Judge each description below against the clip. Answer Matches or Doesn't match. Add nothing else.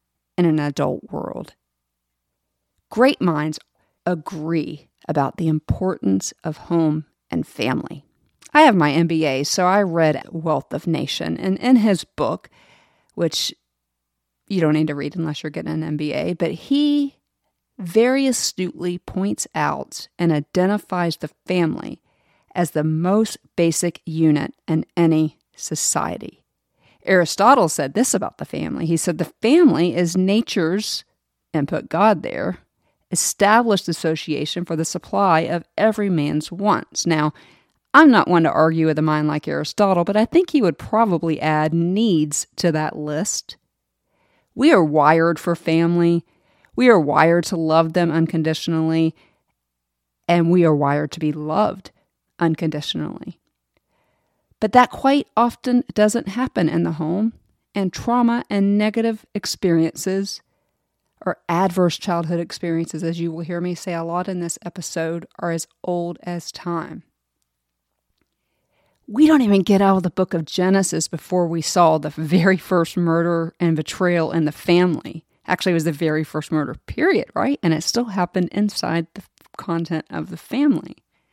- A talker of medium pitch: Matches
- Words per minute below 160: Matches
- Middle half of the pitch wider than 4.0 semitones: Doesn't match